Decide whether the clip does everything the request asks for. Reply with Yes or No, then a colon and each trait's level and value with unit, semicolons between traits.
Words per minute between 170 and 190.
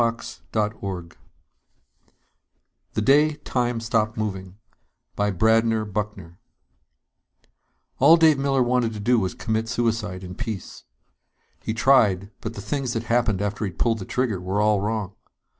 No: slow, 135 wpm